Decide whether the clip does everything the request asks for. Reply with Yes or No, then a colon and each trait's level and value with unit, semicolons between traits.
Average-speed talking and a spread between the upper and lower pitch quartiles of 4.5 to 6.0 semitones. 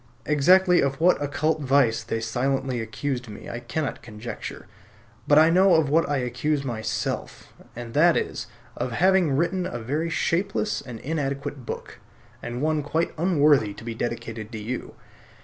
Yes: average, 160 wpm; average, 5.0 semitones